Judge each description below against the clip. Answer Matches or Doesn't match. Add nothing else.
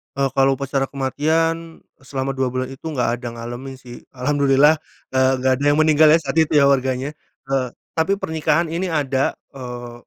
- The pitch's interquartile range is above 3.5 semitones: Doesn't match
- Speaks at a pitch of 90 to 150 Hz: Matches